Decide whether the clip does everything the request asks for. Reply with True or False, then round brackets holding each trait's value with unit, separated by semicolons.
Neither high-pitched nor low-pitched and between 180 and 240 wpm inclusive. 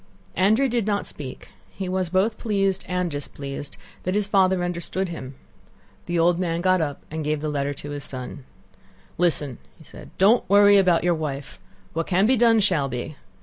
True (175 Hz; 185 wpm)